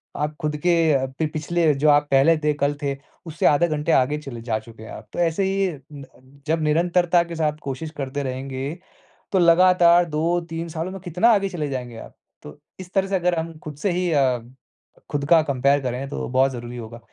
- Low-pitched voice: No, medium, 155 Hz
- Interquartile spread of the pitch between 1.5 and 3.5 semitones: No, average, 3.9 semitones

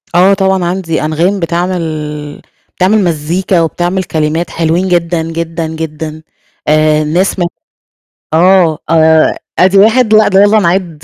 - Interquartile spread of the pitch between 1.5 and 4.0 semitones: Yes, average, 3.0 semitones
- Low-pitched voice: No, medium, 170 Hz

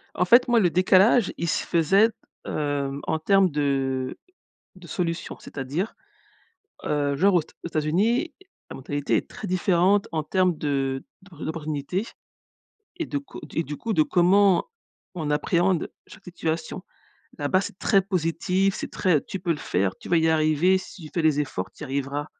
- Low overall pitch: No, medium, 170 Hz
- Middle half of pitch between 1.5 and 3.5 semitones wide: No, average, 4.2 semitones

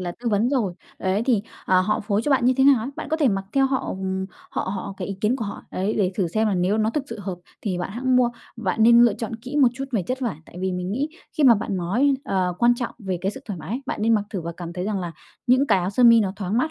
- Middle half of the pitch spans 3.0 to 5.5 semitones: Yes, average, 4.7 semitones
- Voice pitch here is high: Yes, high, 215 Hz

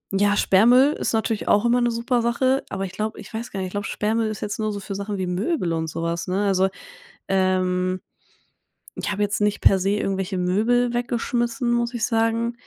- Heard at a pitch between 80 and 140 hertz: No, high, 210 Hz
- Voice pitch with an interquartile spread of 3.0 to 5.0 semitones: Yes, average, 3.7 semitones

